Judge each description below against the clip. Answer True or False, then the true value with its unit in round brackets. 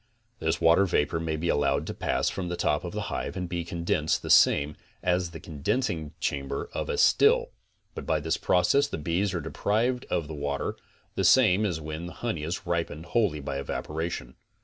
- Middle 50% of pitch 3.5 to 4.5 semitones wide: False (3.1 semitones)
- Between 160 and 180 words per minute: False (200 wpm)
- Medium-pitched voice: False (85 Hz)